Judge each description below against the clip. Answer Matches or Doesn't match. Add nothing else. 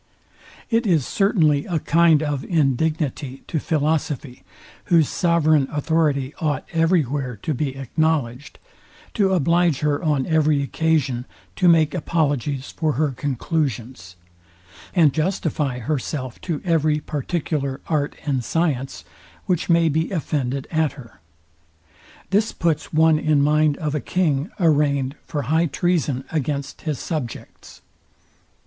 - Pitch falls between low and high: Matches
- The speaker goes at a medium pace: Doesn't match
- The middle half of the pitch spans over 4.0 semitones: Doesn't match